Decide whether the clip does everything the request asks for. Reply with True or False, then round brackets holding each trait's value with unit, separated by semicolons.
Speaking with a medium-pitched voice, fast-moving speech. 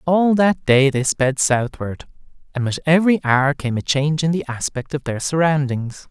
False (145 Hz; 185 wpm)